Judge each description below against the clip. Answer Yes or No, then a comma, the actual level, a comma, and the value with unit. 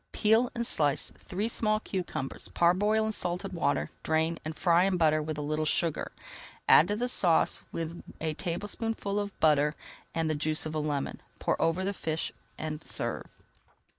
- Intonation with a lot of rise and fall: No, average, 4.6 semitones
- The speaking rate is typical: Yes, average, 170 wpm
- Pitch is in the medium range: Yes, medium, 165 Hz